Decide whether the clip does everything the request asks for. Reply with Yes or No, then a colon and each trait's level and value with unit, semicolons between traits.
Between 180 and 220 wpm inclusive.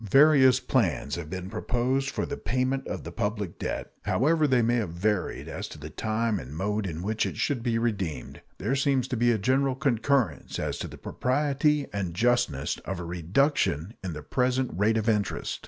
Yes: average, 195 wpm